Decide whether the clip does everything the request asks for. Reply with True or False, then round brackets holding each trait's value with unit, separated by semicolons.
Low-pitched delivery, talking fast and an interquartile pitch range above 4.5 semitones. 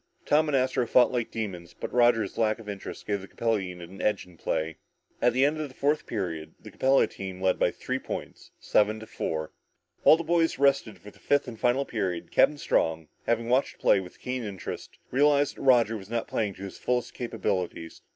True (115 Hz; 220 wpm; 5.2 semitones)